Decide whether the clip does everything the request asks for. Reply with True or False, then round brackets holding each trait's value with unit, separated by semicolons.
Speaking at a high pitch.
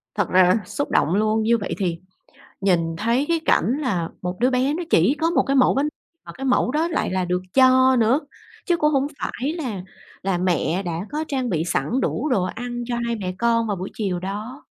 True (230 Hz)